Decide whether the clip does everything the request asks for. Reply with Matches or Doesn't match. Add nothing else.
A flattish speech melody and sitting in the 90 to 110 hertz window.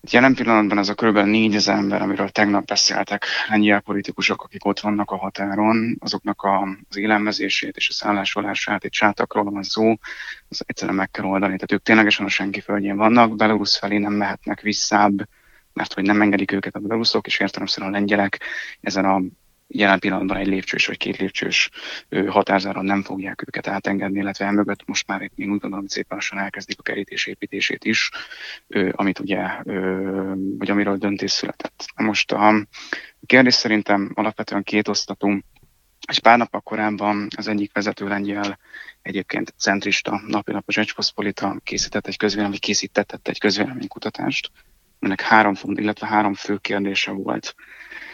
Matches